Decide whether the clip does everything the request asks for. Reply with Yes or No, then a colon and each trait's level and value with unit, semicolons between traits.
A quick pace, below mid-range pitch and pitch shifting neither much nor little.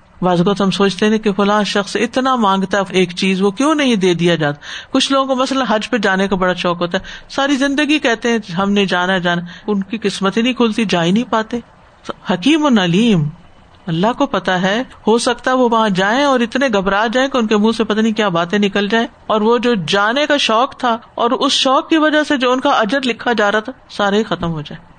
No: fast, 245 wpm; high, 220 Hz; average, 4.5 semitones